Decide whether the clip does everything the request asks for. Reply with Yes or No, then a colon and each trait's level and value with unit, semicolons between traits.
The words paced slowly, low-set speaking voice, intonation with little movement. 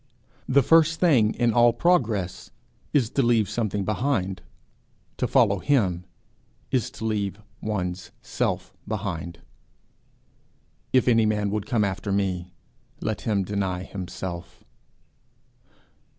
No: slow, 115 wpm; low, 105 Hz; average, 4.1 semitones